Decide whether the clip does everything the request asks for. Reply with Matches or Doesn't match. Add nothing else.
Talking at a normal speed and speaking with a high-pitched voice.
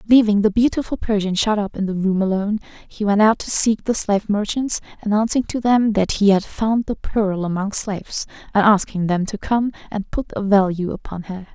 Doesn't match